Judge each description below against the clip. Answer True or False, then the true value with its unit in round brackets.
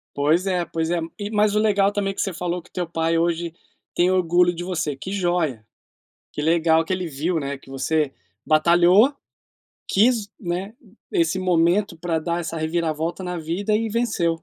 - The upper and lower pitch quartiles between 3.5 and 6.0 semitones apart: False (3.0 semitones)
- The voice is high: False (175 Hz)